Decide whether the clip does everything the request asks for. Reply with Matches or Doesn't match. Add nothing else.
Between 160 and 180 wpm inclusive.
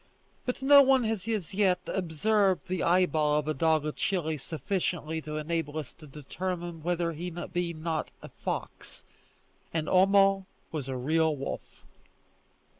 Doesn't match